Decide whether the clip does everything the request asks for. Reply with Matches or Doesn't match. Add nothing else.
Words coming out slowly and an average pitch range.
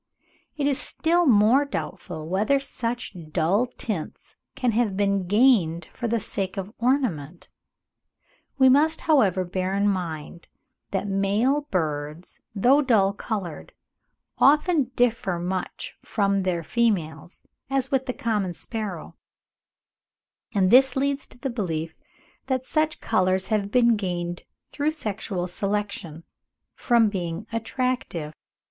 Doesn't match